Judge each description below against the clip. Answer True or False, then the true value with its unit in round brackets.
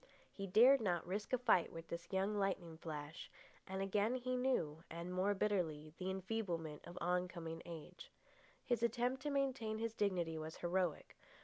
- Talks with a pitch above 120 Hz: True (190 Hz)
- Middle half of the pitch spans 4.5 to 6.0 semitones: True (4.9 semitones)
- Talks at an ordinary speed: True (165 wpm)